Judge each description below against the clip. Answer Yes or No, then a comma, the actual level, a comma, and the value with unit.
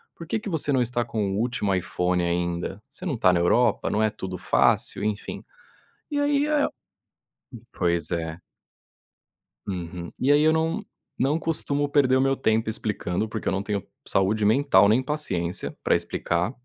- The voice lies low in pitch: Yes, low, 110 Hz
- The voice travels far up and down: Yes, wide, 7.7 semitones